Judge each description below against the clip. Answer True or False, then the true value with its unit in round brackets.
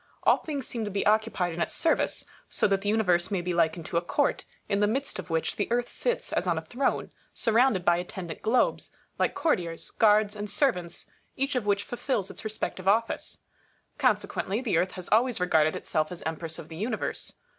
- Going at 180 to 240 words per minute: True (200 wpm)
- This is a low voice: False (200 Hz)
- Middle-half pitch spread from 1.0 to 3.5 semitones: False (4.8 semitones)